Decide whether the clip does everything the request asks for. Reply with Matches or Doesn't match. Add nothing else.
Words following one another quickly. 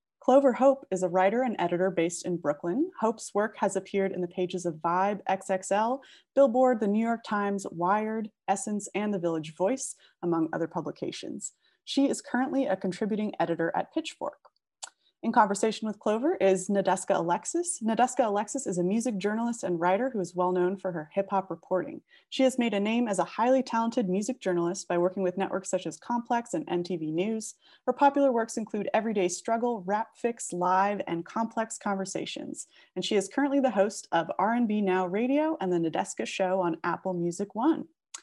Doesn't match